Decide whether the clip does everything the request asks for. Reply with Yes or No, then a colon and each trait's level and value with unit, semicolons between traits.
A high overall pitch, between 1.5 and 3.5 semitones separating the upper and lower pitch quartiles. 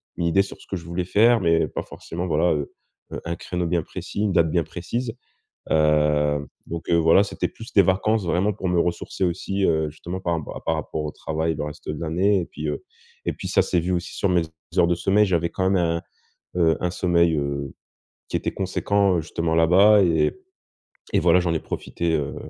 No: very low, 85 Hz; narrow, 2.5 semitones